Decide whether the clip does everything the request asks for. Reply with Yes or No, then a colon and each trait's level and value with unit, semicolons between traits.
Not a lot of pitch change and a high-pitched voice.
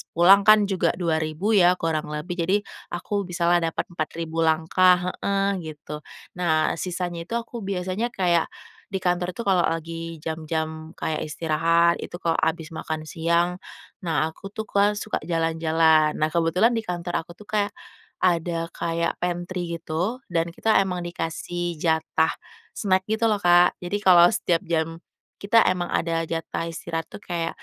No: narrow, 2.2 semitones; medium, 170 Hz